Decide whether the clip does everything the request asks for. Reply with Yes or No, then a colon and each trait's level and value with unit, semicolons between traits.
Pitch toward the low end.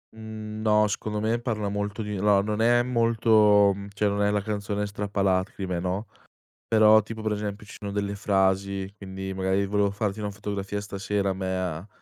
Yes: low, 105 Hz